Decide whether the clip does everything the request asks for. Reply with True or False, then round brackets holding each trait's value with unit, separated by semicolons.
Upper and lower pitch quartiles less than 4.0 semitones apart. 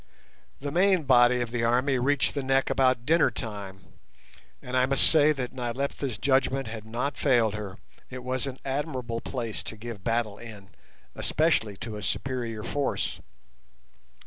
True (3.1 semitones)